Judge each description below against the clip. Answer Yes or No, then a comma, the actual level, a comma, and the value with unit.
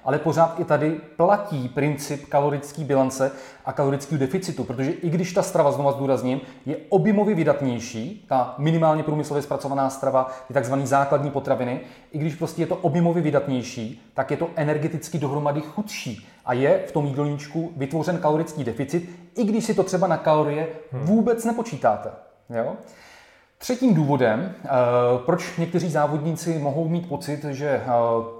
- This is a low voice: No, medium, 150 Hz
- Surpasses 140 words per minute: Yes, average, 150 wpm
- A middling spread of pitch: Yes, average, 3.6 semitones